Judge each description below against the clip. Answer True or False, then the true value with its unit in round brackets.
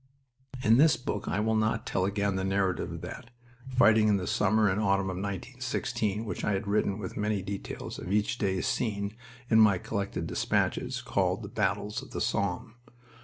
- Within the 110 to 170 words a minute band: False (185 wpm)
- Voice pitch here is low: True (105 Hz)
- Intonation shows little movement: True (2.1 semitones)